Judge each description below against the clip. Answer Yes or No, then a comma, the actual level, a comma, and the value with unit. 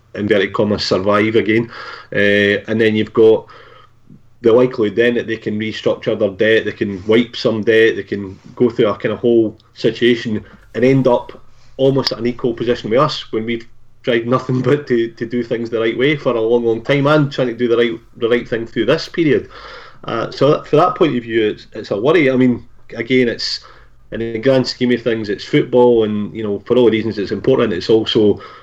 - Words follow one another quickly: Yes, fast, 220 wpm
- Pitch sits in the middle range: No, low, 115 Hz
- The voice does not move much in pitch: Yes, narrow, 1.8 semitones